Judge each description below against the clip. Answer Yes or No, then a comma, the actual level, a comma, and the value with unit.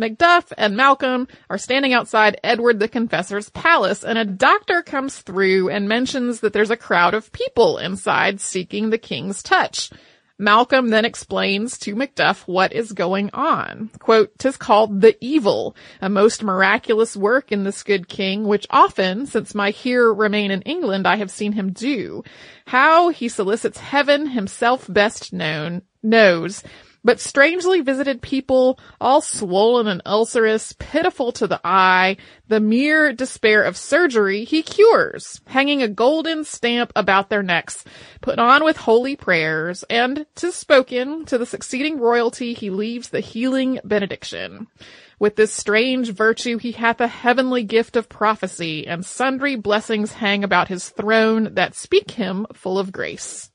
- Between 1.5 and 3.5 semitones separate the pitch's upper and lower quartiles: No, average, 4.5 semitones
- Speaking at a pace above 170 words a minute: No, average, 155 wpm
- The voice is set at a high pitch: Yes, high, 225 Hz